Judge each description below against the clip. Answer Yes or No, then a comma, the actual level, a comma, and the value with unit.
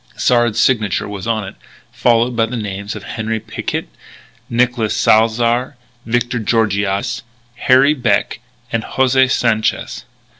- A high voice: No, low, 115 Hz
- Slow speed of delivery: Yes, slow, 120 wpm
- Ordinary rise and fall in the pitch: No, narrow, 2.3 semitones